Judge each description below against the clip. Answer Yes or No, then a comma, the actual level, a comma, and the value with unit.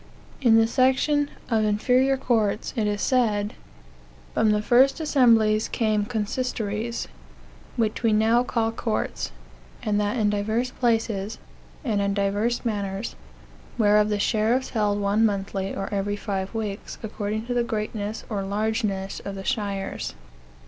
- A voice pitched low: No, high, 215 Hz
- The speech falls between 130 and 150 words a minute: Yes, average, 140 wpm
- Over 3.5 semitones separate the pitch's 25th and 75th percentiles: No, narrow, 2.4 semitones